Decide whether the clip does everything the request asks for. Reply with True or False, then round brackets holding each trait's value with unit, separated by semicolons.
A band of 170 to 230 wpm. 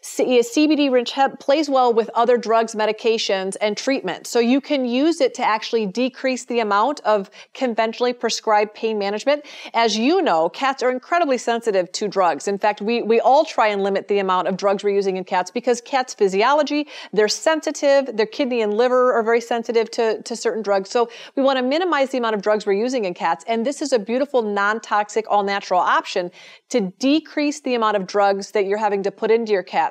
True (200 wpm)